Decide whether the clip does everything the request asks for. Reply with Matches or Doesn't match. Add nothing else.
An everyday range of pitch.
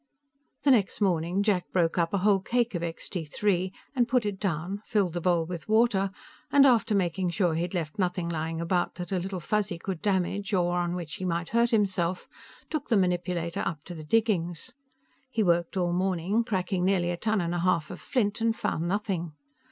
Matches